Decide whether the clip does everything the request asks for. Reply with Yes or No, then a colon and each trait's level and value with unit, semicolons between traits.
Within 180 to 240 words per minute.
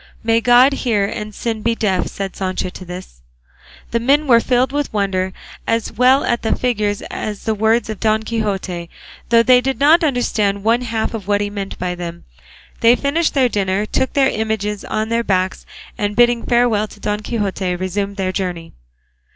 Yes: average, 190 wpm